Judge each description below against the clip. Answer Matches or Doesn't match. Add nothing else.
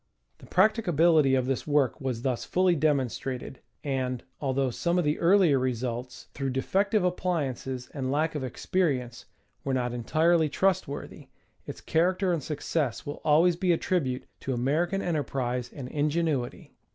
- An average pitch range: Matches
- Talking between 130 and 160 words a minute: Matches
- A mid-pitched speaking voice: Matches